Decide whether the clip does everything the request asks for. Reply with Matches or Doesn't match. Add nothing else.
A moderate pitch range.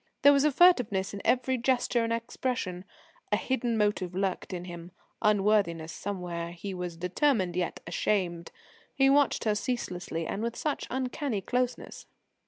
Doesn't match